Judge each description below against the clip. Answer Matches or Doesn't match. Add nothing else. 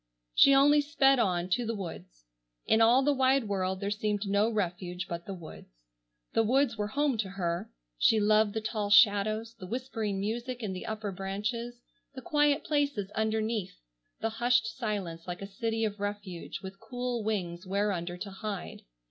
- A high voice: Matches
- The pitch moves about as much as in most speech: Matches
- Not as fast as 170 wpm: Doesn't match